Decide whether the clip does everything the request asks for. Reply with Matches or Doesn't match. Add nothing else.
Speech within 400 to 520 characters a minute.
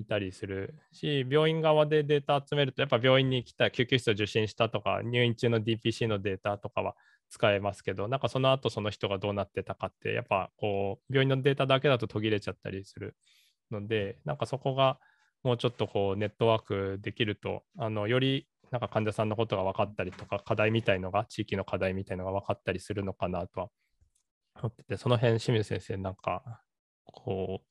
Matches